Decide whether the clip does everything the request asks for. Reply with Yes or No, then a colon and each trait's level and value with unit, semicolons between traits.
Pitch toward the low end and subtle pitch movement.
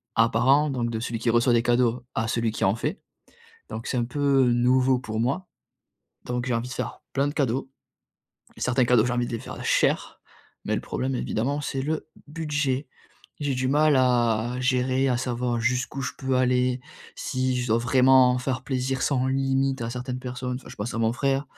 Yes: low, 125 Hz; narrow, 1.9 semitones